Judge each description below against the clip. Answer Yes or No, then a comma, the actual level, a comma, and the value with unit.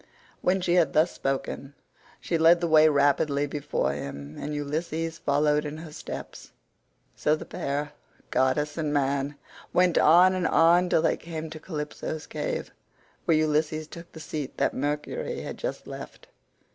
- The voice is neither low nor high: Yes, medium, 155 Hz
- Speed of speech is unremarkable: Yes, average, 160 wpm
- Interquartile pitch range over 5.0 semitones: No, narrow, 2.4 semitones